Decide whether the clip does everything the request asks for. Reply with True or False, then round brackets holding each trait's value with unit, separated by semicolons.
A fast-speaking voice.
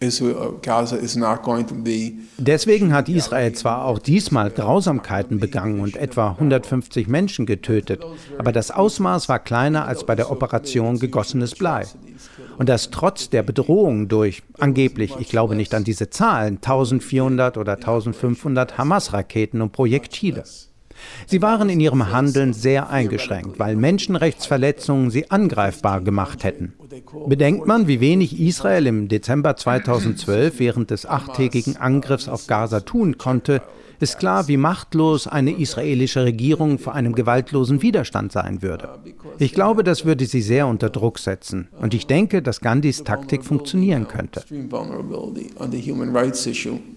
False (130 wpm)